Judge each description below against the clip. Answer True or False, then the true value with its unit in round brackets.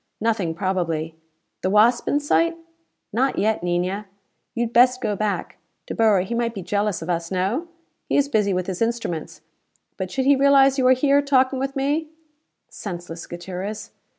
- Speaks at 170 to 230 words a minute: True (180 wpm)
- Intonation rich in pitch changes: True (6.3 semitones)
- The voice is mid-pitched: False (220 Hz)